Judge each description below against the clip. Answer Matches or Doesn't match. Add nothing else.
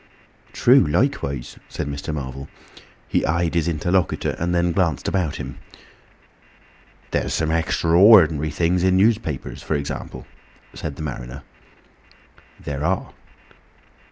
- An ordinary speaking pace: Doesn't match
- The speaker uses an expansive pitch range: Doesn't match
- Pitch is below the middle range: Matches